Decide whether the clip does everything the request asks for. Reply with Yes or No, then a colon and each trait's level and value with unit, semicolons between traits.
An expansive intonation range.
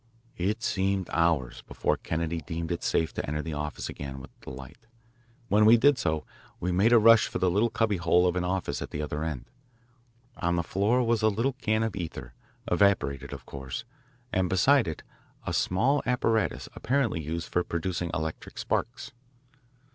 Yes: wide, 5.7 semitones